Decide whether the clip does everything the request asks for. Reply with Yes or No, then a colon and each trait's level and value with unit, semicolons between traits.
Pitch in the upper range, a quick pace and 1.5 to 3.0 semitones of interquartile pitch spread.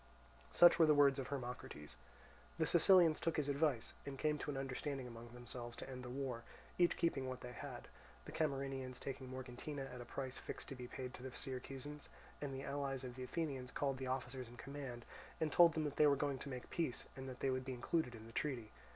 No: low, 135 Hz; fast, 220 wpm; narrow, 2.4 semitones